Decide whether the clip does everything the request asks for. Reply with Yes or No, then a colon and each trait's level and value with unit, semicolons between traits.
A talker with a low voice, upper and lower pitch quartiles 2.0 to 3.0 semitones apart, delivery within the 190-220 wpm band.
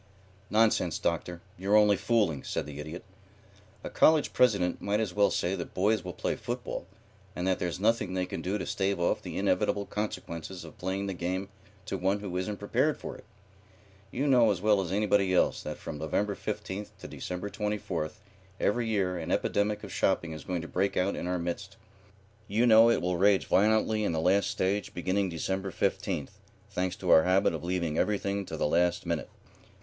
Yes: very low, 95 Hz; average, 2.7 semitones; average, 195 wpm